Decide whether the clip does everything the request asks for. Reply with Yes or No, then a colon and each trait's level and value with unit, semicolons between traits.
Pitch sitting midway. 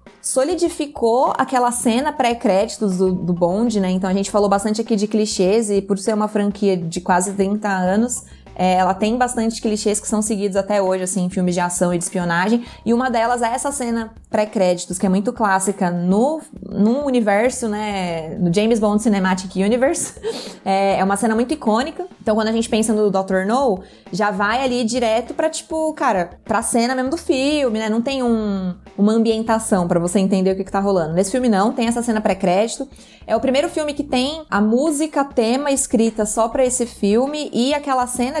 No: high, 220 Hz